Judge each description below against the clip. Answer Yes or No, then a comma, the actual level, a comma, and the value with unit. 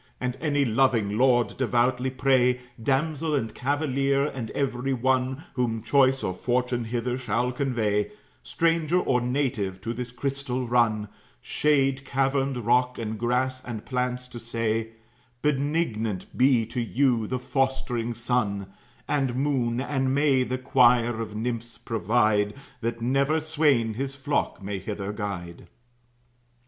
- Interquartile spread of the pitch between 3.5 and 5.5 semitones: No, average, 2.9 semitones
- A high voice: No, low, 125 Hz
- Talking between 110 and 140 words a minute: Yes, slow, 135 wpm